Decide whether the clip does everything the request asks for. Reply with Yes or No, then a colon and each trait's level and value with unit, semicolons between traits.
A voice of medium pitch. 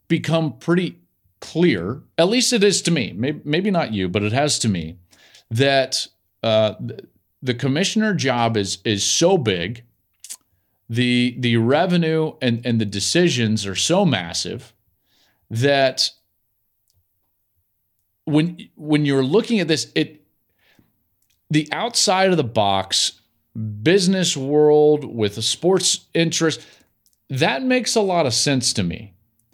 No: low, 130 Hz